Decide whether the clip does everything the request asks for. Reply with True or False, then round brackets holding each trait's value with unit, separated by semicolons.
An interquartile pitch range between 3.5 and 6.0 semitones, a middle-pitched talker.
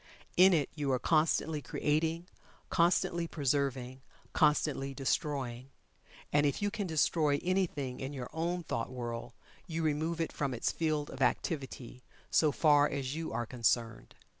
True (3.8 semitones; 145 Hz)